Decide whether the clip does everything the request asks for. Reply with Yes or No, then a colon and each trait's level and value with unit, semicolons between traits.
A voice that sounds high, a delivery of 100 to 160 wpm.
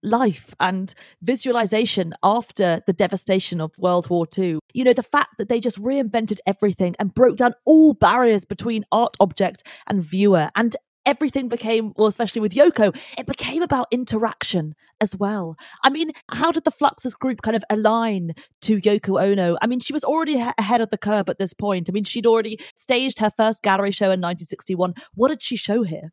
No: high, 215 Hz; average, 195 wpm